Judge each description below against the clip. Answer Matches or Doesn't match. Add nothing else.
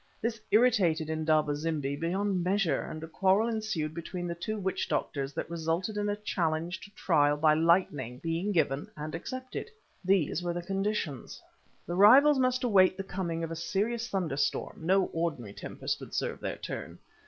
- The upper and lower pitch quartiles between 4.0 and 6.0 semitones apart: Matches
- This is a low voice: Doesn't match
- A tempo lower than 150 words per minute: Doesn't match